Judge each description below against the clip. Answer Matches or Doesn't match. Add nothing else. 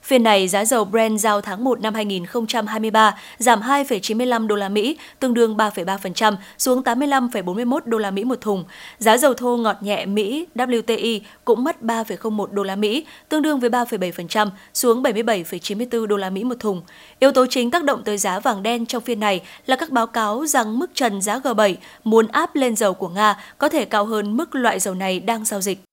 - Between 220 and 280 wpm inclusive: Doesn't match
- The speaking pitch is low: Doesn't match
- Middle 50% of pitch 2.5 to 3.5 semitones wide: Matches